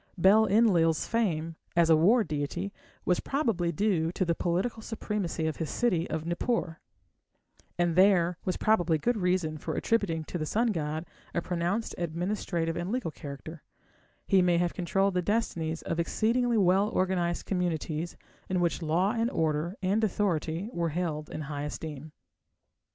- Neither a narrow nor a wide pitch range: Yes, average, 3.8 semitones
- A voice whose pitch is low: No, medium, 175 Hz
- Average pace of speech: Yes, average, 155 wpm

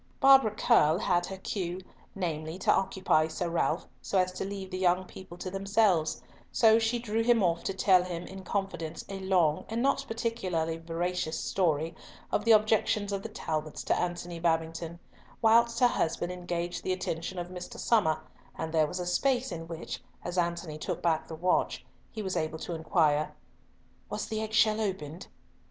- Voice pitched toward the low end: No, medium, 180 Hz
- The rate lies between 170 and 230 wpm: Yes, average, 180 wpm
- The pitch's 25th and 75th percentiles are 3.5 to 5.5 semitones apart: Yes, average, 3.9 semitones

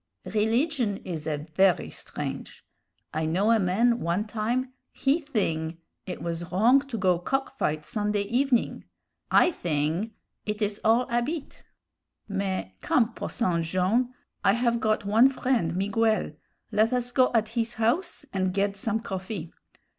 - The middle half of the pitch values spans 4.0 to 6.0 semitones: Yes, average, 4.5 semitones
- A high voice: Yes, high, 215 Hz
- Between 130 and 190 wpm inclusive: Yes, average, 145 wpm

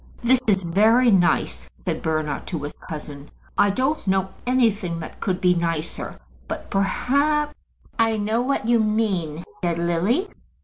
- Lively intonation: Yes, wide, 5.8 semitones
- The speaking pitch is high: Yes, high, 195 Hz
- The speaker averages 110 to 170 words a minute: Yes, average, 150 wpm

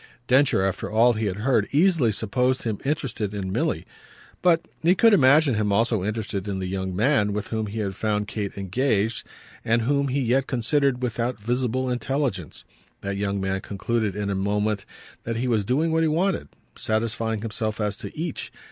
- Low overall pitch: Yes, low, 110 Hz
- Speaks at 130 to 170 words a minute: No, average, 185 wpm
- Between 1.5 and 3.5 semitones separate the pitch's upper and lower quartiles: No, average, 4.3 semitones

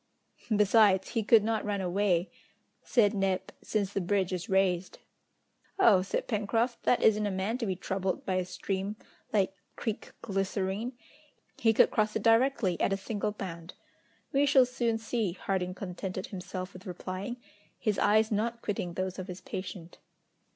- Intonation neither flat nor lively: Yes, average, 3.0 semitones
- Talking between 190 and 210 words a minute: No, average, 160 wpm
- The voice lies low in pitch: No, high, 200 Hz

